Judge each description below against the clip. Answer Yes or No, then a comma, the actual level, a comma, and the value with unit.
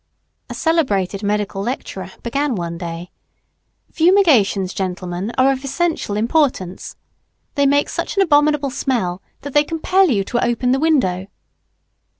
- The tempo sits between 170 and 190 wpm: No, slow, 135 wpm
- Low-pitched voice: No, very high, 250 Hz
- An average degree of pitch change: No, wide, 7.3 semitones